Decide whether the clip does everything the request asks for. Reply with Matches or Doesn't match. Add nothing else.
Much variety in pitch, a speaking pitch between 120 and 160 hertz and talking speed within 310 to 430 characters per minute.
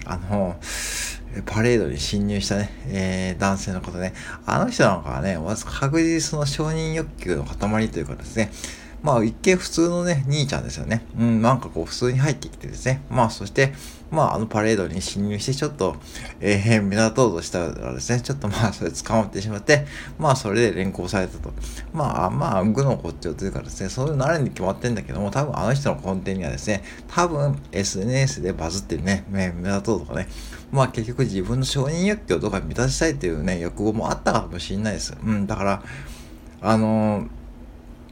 Doesn't match